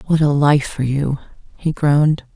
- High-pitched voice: No, medium, 145 Hz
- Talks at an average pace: Yes, average, 180 wpm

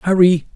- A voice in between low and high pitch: Yes, medium, 180 Hz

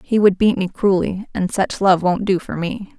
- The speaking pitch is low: No, high, 190 Hz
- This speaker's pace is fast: Yes, fast, 240 wpm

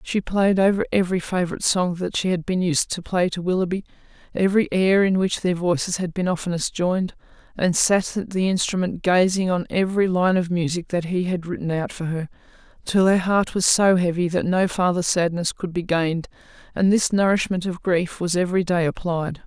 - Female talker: Yes, female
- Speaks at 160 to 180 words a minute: No, average, 200 wpm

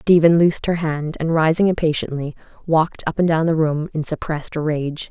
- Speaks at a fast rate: No, average, 190 wpm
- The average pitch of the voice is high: No, medium, 160 Hz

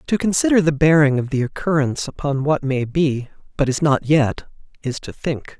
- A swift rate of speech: No, average, 195 wpm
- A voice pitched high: No, medium, 145 Hz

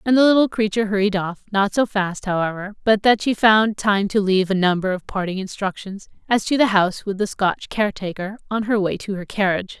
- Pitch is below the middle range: No, high, 200 Hz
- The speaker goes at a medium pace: No, fast, 220 wpm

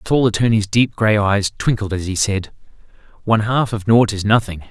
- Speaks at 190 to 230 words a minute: Yes, fast, 205 wpm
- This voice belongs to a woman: No, male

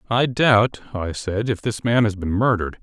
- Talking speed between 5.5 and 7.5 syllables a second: No, 4.8 syllables/s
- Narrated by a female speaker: No, male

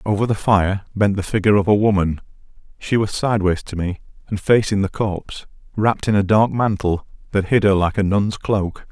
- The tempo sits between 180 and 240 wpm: Yes, average, 200 wpm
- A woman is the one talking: No, male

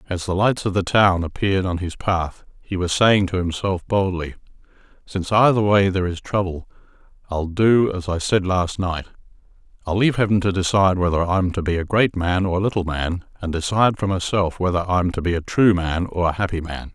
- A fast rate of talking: Yes, fast, 210 wpm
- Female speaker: No, male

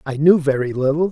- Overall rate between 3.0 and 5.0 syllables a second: No, 6.1 syllables/s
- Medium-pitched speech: Yes, medium, 150 Hz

